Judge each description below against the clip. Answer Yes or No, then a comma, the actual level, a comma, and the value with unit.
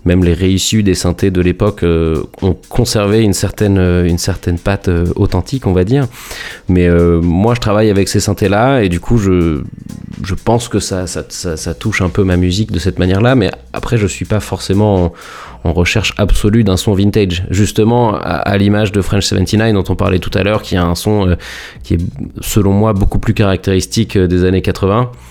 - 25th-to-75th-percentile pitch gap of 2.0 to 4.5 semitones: Yes, average, 2.9 semitones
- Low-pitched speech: Yes, low, 100 Hz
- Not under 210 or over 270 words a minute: Yes, average, 215 wpm